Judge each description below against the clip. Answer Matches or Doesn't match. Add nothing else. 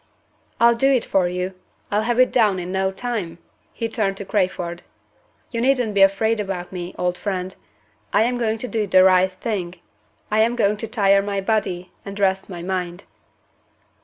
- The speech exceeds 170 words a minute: Matches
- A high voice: Matches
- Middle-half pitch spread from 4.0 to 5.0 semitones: Doesn't match